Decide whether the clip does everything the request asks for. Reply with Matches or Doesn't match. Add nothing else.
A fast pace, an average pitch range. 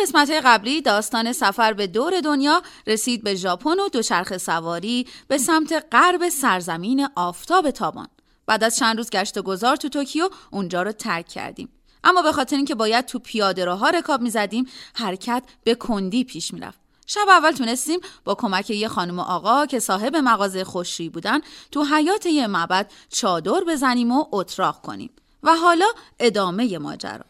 Doesn't match